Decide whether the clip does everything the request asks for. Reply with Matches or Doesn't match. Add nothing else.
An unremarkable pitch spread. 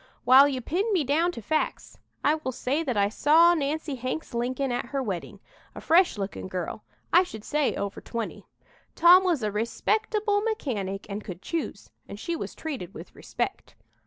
Doesn't match